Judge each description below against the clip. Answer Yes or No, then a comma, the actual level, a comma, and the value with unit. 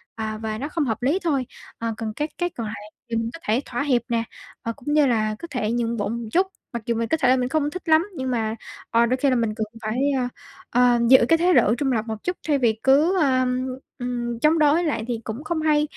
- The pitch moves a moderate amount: Yes, average, 4.6 semitones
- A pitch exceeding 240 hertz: Yes, very high, 250 Hz